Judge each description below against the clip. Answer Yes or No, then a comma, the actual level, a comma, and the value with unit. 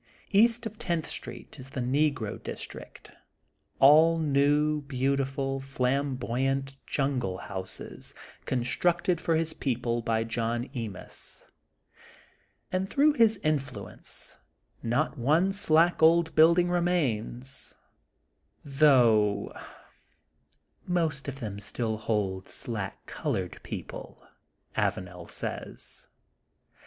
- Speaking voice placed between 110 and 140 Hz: Yes, low, 135 Hz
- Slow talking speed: Yes, slow, 100 wpm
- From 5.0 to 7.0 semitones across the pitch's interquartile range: Yes, wide, 5.4 semitones